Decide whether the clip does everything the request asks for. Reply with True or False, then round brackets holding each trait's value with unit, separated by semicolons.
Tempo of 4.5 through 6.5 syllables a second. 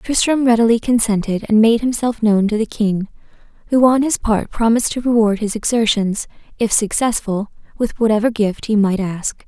True (5.1 syllables/s)